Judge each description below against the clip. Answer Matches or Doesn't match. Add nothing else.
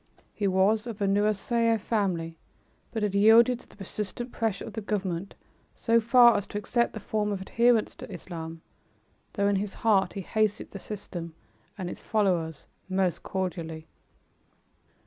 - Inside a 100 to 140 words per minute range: Doesn't match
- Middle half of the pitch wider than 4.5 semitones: Doesn't match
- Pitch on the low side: Doesn't match